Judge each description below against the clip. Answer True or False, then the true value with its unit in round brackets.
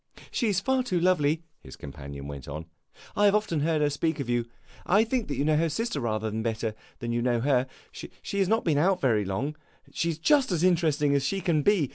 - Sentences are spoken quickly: True (225 wpm)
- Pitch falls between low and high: True (150 Hz)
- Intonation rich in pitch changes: True (7.6 semitones)